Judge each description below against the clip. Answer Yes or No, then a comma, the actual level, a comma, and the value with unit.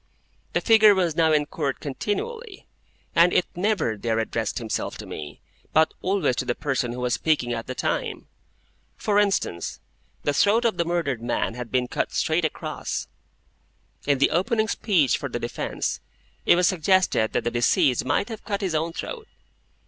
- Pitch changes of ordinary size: No, wide, 8.3 semitones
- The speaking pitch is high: No, medium, 160 Hz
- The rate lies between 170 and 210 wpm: Yes, average, 175 wpm